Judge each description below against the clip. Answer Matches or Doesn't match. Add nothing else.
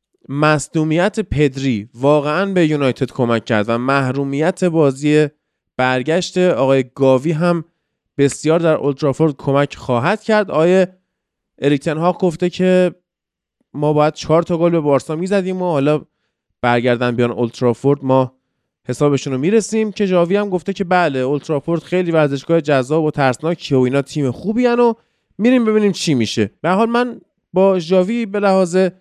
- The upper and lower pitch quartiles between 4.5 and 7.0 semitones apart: Matches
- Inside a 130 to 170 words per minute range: Matches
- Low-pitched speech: Doesn't match